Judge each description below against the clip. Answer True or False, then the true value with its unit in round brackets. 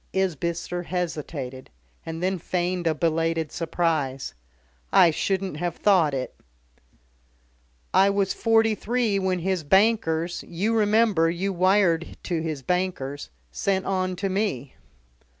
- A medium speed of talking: False (120 wpm)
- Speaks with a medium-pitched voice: True (180 Hz)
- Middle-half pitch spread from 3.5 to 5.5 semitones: False (3.1 semitones)